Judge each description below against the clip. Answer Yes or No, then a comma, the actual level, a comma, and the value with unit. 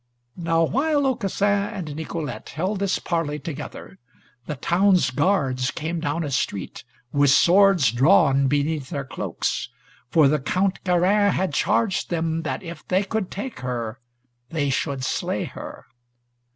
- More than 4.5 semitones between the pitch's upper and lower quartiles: Yes, average, 5.2 semitones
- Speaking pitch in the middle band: Yes, medium, 165 Hz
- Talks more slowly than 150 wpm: Yes, average, 140 wpm